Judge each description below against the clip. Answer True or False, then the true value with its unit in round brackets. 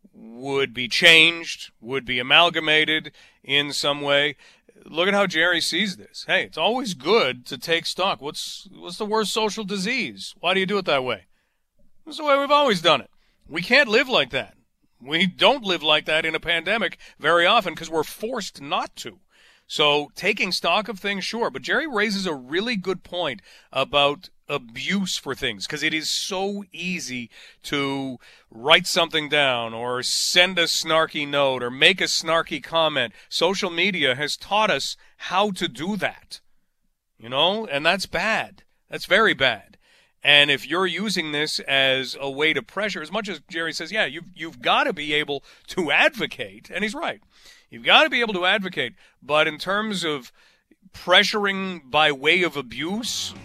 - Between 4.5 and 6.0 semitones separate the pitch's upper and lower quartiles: True (5.0 semitones)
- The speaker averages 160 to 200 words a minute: True (175 wpm)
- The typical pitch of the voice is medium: True (165 Hz)